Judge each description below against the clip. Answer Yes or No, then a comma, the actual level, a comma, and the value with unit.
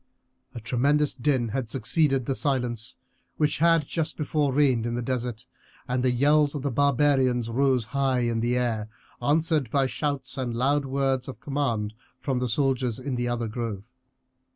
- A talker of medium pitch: No, low, 130 Hz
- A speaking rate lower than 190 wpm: Yes, average, 170 wpm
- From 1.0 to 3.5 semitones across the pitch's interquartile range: Yes, average, 3.0 semitones